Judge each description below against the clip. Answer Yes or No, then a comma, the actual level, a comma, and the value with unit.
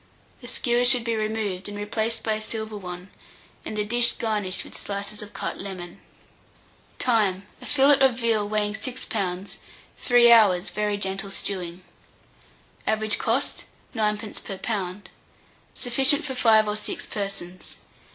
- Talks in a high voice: Yes, high, 215 Hz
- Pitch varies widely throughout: No, average, 2.8 semitones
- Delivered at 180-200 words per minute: No, average, 145 wpm